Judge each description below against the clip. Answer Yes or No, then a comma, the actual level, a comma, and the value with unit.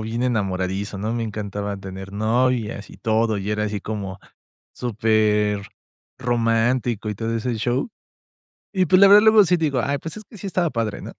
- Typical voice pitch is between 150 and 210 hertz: No, low, 115 Hz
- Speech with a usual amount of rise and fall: Yes, average, 3.6 semitones